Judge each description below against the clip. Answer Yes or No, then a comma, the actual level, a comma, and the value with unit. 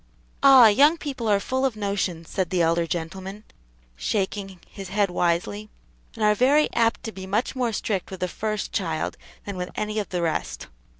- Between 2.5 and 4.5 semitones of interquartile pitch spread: Yes, average, 3.5 semitones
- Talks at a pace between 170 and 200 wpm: Yes, average, 185 wpm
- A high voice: Yes, high, 200 Hz